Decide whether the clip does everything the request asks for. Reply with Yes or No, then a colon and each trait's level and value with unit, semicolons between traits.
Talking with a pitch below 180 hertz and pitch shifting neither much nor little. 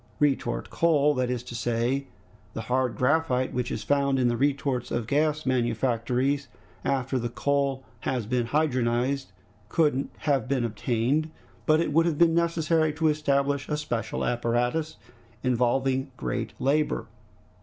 Yes: low, 135 Hz; average, 3.4 semitones